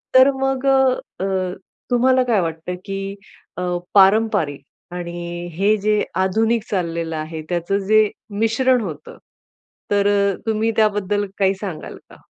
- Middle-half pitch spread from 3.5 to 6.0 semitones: Yes, average, 4.4 semitones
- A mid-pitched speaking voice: No, high, 200 Hz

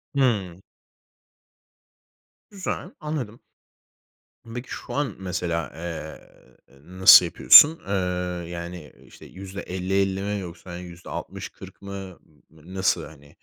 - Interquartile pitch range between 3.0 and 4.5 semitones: No, narrow, 2.4 semitones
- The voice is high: No, very low, 95 Hz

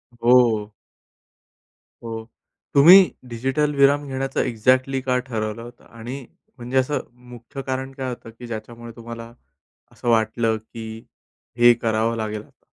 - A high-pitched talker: No, low, 120 Hz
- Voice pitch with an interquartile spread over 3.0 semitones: No, narrow, 2.5 semitones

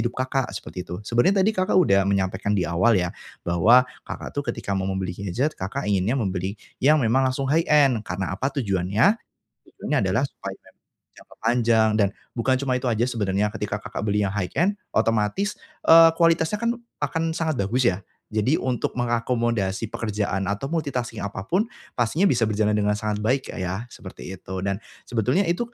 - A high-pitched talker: No, low, 115 Hz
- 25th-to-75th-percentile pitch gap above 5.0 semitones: Yes, wide, 5.4 semitones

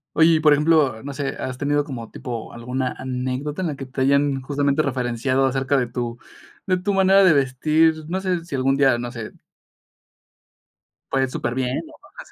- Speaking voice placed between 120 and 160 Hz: Yes, low, 135 Hz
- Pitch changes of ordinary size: Yes, average, 3.0 semitones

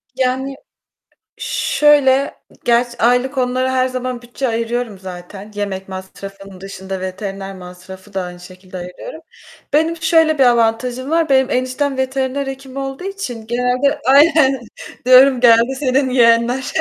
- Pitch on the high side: Yes, very high, 250 Hz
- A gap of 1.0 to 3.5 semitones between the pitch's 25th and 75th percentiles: No, average, 5.1 semitones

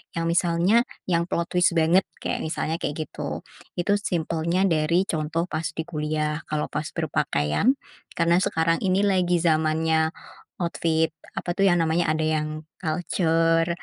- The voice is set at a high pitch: No, medium, 165 Hz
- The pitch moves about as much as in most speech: No, narrow, 1.9 semitones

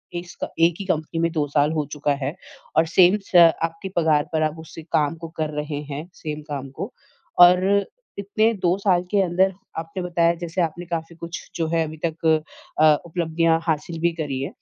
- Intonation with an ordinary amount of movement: No, narrow, 2.1 semitones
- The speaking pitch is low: No, medium, 165 Hz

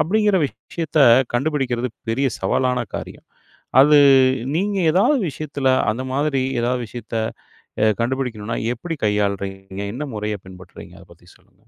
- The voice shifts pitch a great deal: Yes, wide, 6.2 semitones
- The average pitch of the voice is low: Yes, low, 125 Hz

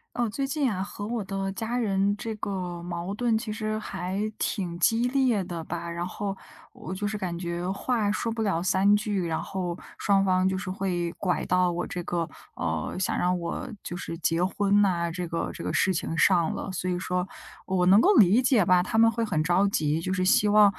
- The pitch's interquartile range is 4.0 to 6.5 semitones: No, average, 3.0 semitones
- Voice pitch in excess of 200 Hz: No, high, 190 Hz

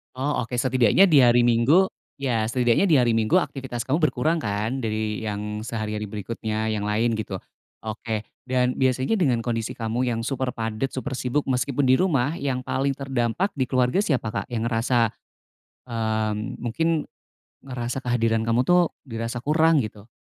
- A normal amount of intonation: Yes, average, 3.1 semitones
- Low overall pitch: Yes, low, 120 Hz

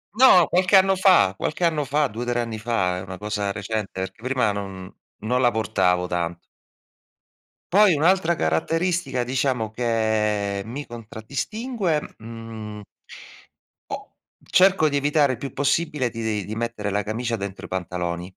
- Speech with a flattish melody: No, wide, 6.2 semitones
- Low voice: Yes, low, 115 Hz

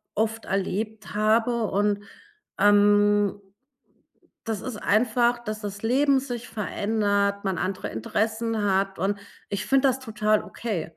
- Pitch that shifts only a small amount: Yes, narrow, 2.0 semitones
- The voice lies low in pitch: No, high, 210 Hz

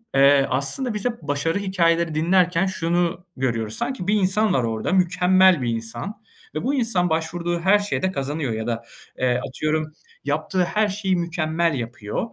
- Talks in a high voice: No, medium, 170 Hz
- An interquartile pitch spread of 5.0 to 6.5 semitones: Yes, wide, 5.4 semitones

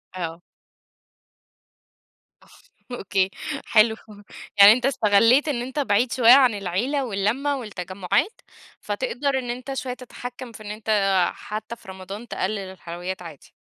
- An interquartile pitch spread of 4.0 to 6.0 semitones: Yes, average, 4.7 semitones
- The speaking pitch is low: No, high, 220 Hz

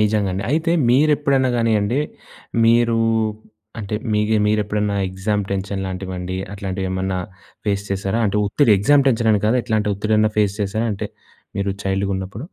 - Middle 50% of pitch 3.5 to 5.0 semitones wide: No, average, 2.7 semitones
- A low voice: Yes, low, 105 Hz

